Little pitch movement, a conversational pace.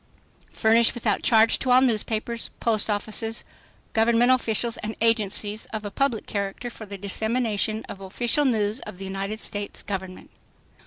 Yes: narrow, 2.3 semitones; average, 150 wpm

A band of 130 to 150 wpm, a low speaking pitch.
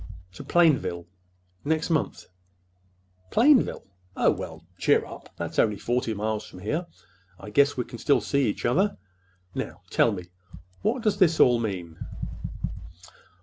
Yes: slow, 135 wpm; low, 120 Hz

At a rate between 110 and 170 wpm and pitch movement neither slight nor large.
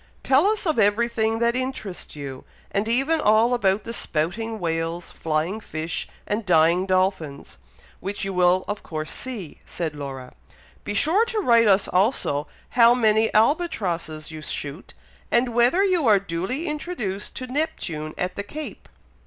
No: average, 155 wpm; wide, 6.4 semitones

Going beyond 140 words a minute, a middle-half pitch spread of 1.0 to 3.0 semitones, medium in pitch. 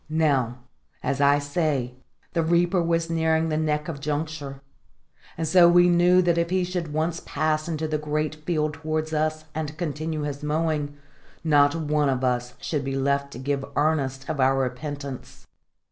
Yes: average, 170 wpm; narrow, 2.4 semitones; medium, 155 Hz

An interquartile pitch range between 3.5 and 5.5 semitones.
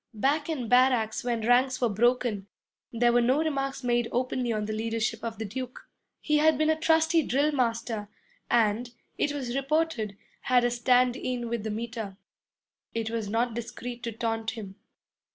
No: narrow, 2.6 semitones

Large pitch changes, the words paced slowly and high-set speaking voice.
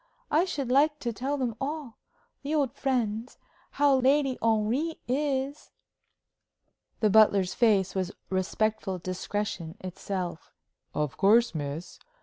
Yes: wide, 6.3 semitones; slow, 120 wpm; high, 230 Hz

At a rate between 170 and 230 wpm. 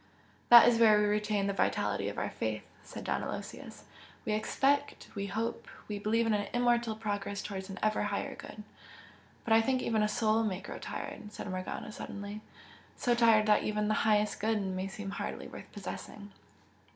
Yes: average, 190 wpm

